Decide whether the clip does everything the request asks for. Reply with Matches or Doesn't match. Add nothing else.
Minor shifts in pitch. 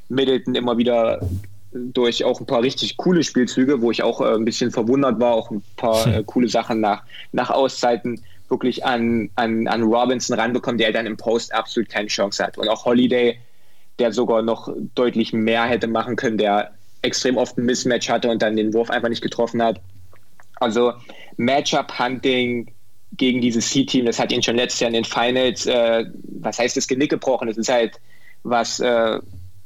Matches